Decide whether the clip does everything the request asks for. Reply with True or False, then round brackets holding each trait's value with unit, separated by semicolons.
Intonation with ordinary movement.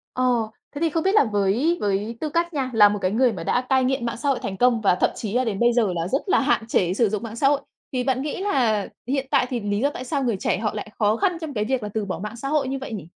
True (4.7 semitones)